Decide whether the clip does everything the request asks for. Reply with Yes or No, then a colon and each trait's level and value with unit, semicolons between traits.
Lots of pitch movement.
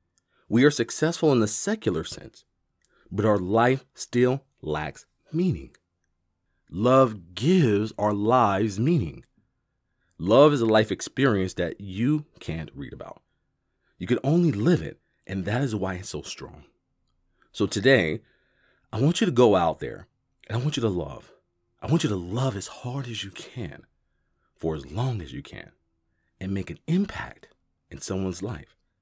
Yes: wide, 6.6 semitones